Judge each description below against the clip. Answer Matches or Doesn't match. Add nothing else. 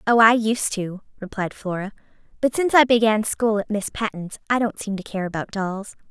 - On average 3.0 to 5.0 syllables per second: Doesn't match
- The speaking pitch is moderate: Doesn't match